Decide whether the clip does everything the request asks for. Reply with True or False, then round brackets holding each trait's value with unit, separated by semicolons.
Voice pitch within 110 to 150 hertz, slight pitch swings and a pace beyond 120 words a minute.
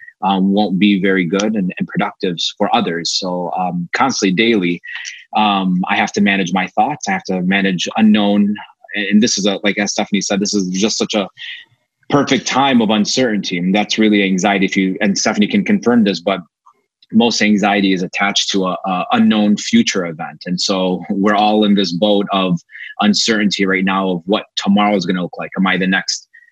False (100 Hz; 1.9 semitones; 200 wpm)